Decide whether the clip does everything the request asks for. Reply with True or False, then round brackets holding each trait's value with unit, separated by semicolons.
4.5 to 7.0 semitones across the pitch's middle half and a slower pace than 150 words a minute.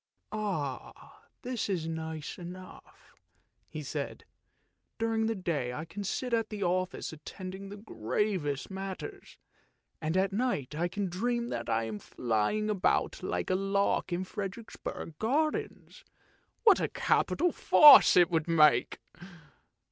True (5.2 semitones; 140 wpm)